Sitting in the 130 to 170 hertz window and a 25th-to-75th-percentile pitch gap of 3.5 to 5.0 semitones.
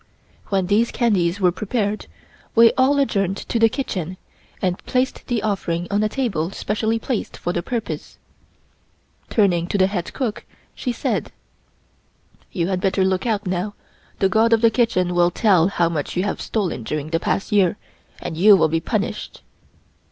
No: high, 200 Hz; average, 4.1 semitones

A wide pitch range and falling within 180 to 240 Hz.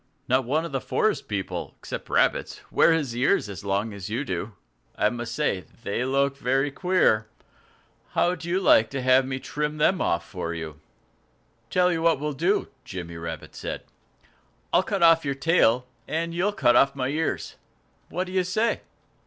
No: wide, 7.2 semitones; low, 135 Hz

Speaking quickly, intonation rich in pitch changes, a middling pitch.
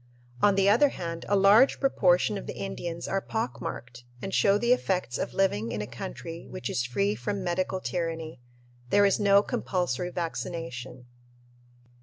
No: average, 165 wpm; wide, 7.4 semitones; medium, 180 Hz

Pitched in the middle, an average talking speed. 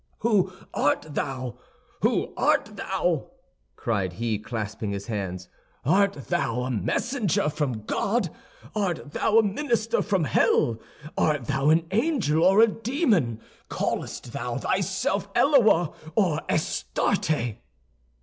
No: medium, 150 Hz; slow, 120 wpm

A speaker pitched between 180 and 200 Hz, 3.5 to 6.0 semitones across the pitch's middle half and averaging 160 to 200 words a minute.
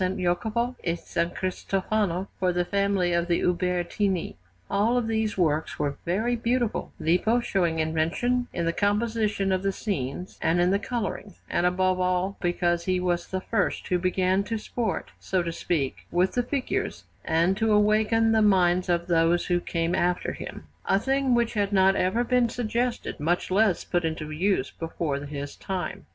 Yes: medium, 185 Hz; average, 3.8 semitones; average, 170 wpm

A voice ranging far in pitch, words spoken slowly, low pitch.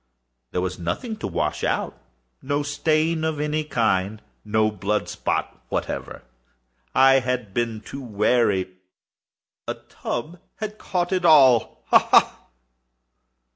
Yes: wide, 7.2 semitones; slow, 115 wpm; low, 120 Hz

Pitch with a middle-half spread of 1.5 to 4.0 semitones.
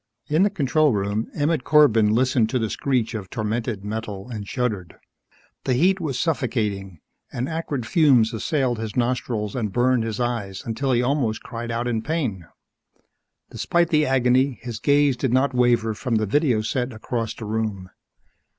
Yes: average, 3.4 semitones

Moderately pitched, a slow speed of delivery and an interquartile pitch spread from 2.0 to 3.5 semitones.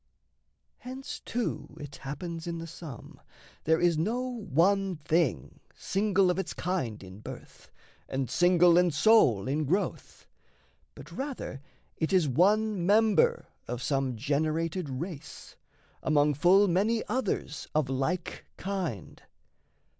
No: medium, 170 Hz; slow, 125 wpm; average, 5.3 semitones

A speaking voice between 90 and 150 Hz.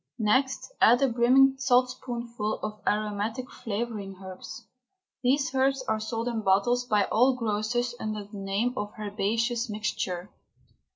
No: high, 230 Hz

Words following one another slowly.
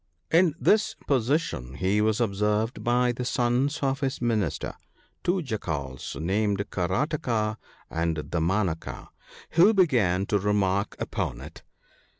Yes: slow, 120 wpm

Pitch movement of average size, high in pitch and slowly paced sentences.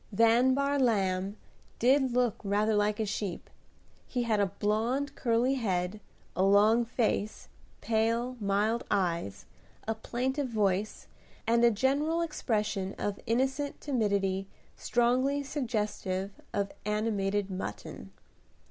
Yes: average, 3.8 semitones; high, 220 Hz; slow, 115 wpm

